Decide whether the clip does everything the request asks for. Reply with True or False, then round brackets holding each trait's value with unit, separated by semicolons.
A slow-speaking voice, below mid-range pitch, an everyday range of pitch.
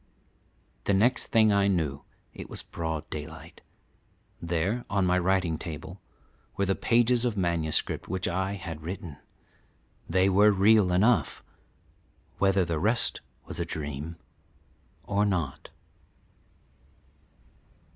True (115 wpm; 95 Hz; 3.7 semitones)